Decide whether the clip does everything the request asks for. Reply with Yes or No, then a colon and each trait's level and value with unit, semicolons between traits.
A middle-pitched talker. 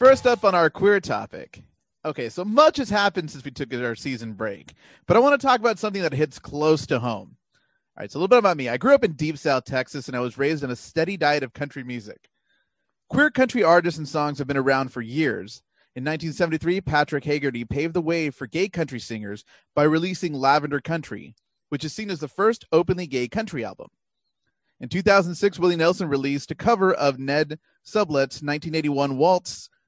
Yes: medium, 155 Hz